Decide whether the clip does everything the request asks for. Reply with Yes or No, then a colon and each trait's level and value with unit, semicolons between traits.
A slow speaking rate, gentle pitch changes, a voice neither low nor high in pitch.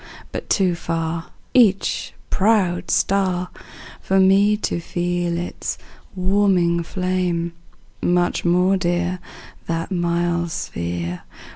Yes: slow, 100 wpm; narrow, 1.8 semitones; medium, 175 Hz